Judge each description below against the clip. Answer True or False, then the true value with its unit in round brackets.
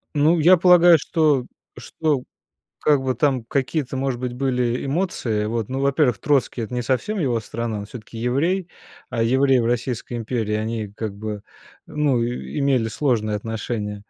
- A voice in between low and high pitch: False (125 Hz)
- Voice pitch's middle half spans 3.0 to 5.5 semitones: True (4.0 semitones)